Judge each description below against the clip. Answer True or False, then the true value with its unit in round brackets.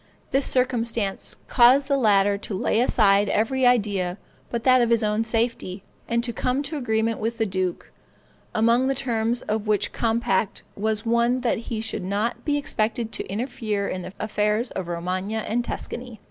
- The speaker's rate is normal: True (175 wpm)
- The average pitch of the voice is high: True (225 Hz)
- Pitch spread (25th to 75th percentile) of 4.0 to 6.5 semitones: False (2.8 semitones)